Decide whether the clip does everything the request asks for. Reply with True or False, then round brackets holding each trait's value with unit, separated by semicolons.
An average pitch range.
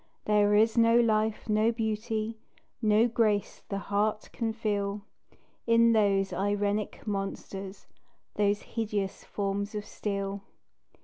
False (1.6 semitones)